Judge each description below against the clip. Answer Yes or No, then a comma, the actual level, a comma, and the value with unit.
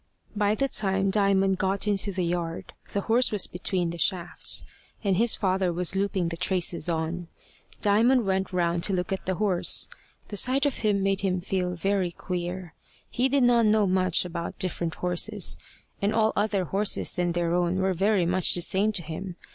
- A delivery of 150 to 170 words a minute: No, average, 185 wpm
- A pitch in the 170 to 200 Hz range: Yes, high, 190 Hz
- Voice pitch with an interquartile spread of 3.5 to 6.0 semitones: No, narrow, 2.5 semitones